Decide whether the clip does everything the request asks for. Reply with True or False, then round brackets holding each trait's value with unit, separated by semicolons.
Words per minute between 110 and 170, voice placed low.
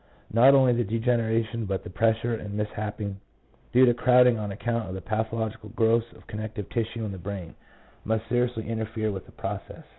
False (185 wpm; 110 Hz)